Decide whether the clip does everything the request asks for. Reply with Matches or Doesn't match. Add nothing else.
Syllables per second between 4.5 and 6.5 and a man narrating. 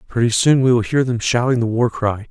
Matches